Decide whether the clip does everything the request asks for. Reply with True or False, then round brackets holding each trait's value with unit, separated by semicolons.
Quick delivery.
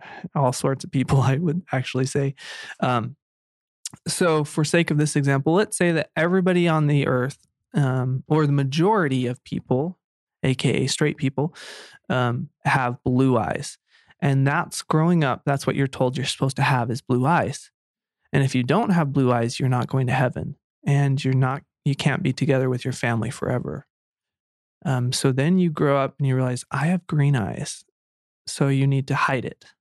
False (185 wpm)